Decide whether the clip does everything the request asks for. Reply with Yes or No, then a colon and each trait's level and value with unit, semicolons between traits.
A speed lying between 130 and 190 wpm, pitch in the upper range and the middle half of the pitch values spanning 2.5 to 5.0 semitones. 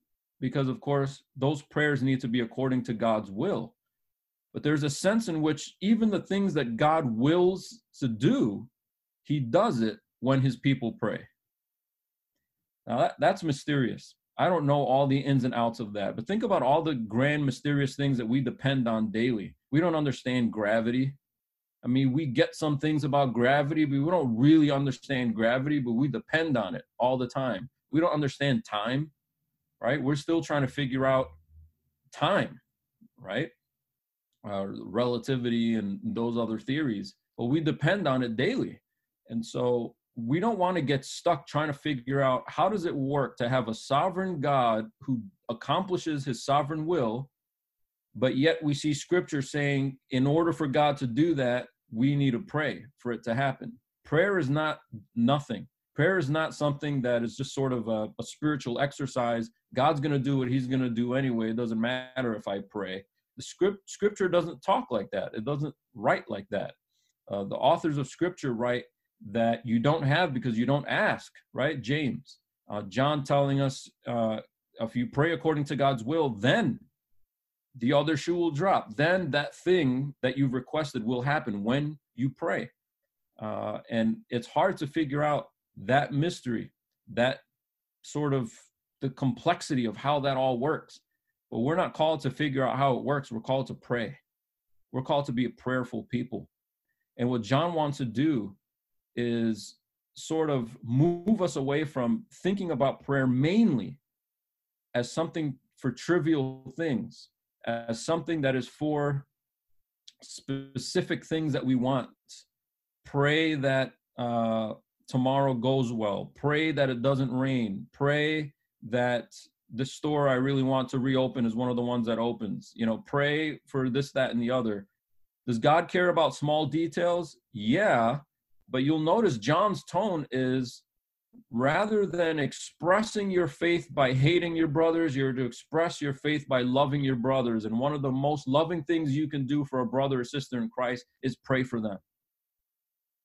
No: average, 170 wpm; low, 135 Hz; average, 3.8 semitones